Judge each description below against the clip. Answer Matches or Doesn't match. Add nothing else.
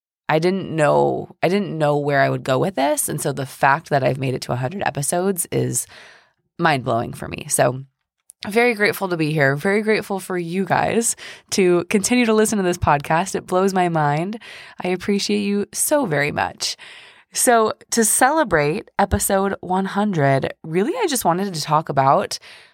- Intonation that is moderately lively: Doesn't match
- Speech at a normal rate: Matches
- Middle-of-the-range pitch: Matches